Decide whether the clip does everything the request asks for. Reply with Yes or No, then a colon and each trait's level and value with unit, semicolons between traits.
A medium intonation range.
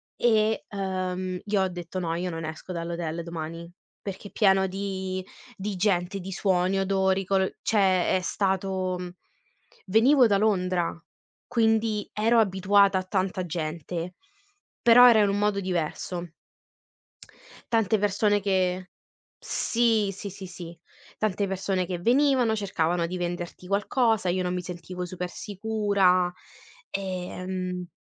No: narrow, 2.2 semitones